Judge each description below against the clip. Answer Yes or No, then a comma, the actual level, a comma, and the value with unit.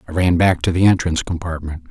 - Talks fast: Yes, fast, 220 wpm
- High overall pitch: No, very low, 85 Hz